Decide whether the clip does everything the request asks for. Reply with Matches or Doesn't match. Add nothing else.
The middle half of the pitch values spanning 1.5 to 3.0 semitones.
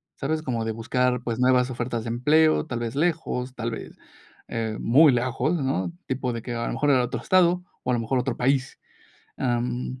Matches